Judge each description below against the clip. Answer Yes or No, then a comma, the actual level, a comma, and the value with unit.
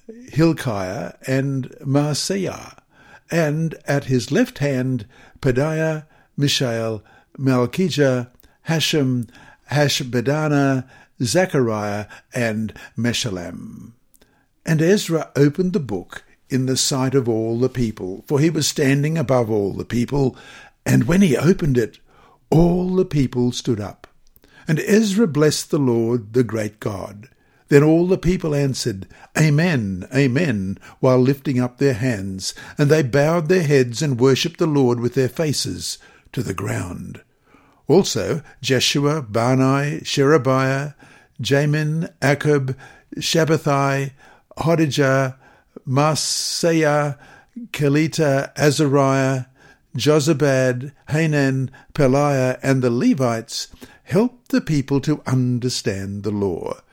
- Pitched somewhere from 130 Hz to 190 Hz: Yes, low, 135 Hz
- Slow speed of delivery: Yes, slow, 110 wpm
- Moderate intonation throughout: Yes, average, 3.5 semitones